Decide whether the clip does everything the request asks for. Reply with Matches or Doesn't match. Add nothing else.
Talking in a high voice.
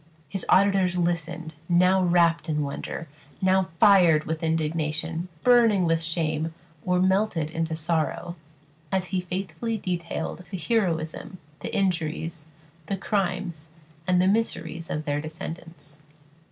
Doesn't match